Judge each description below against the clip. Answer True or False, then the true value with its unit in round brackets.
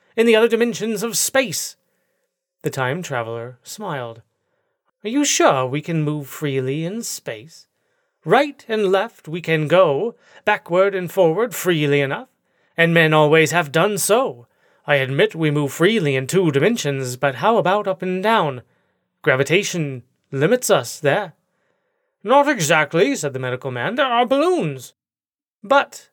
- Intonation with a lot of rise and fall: True (7.9 semitones)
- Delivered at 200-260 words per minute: False (145 wpm)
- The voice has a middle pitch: True (180 Hz)